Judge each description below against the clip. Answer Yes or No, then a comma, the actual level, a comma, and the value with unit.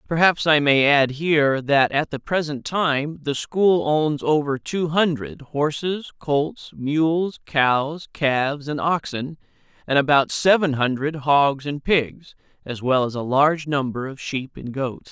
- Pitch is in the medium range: Yes, medium, 145 Hz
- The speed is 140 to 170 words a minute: Yes, average, 160 wpm